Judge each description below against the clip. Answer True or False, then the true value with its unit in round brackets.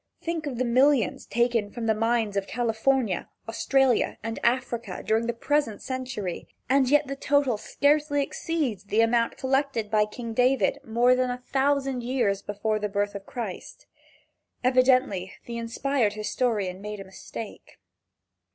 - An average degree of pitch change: True (3.9 semitones)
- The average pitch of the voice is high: True (235 Hz)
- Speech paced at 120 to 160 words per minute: True (150 wpm)